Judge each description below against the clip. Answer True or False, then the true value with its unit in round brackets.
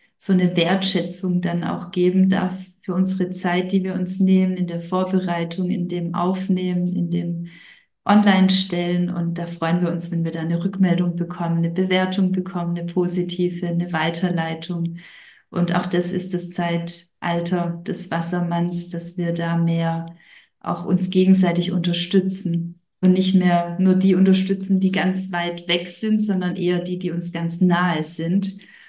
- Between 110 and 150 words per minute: False (160 wpm)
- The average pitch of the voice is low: False (180 Hz)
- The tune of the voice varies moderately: False (1.4 semitones)